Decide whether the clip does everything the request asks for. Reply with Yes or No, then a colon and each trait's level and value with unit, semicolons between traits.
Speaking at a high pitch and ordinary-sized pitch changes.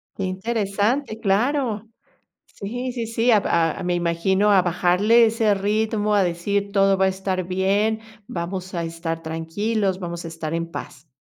Yes: high, 195 Hz; average, 3.8 semitones